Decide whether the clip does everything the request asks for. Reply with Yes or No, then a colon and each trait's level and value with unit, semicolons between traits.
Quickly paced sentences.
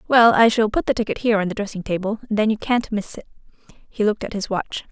Yes: fast, 270 wpm